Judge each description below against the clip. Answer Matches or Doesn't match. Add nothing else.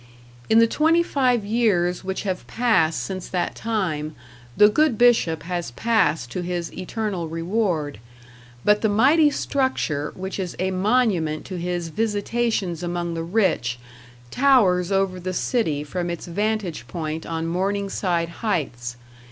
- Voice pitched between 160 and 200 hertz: Matches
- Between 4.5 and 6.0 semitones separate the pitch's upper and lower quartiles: Matches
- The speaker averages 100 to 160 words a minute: Matches